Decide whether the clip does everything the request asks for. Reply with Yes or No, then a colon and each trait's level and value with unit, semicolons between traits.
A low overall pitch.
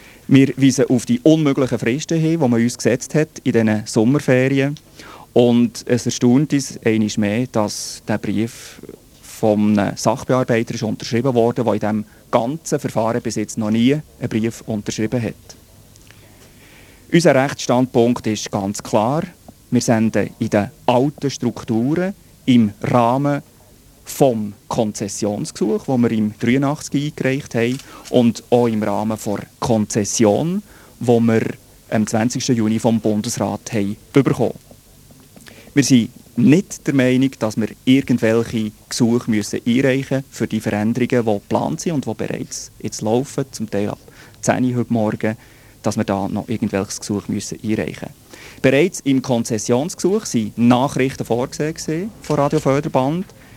Yes: low, 120 Hz